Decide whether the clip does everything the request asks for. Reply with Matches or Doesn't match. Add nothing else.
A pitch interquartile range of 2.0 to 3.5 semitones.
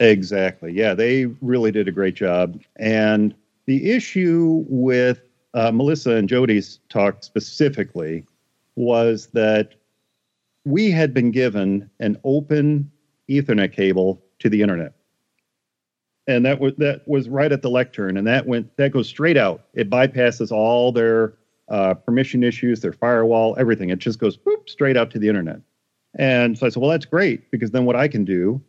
Doesn't match